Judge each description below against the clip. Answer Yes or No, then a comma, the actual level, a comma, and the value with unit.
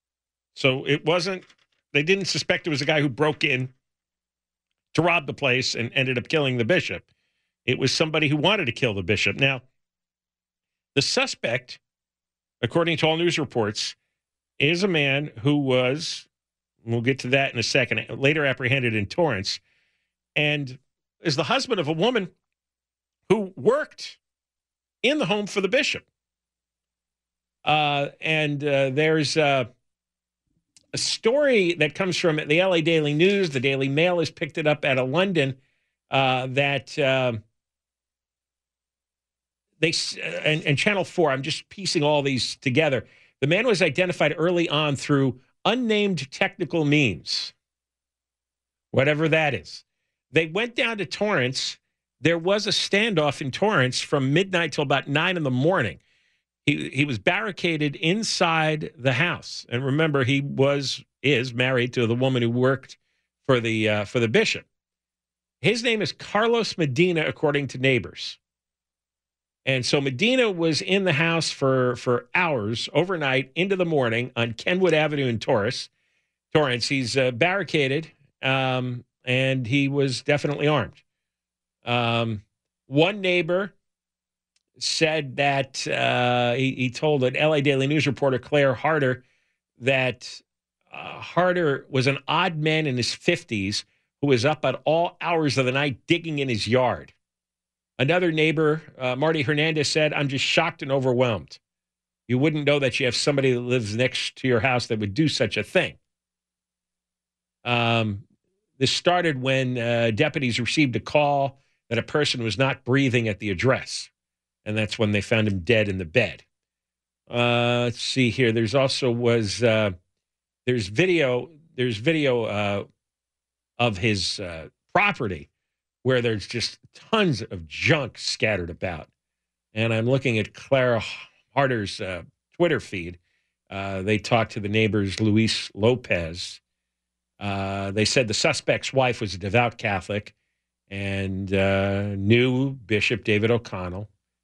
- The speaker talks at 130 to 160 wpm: Yes, average, 150 wpm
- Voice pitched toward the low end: Yes, low, 130 Hz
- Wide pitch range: Yes, wide, 6.8 semitones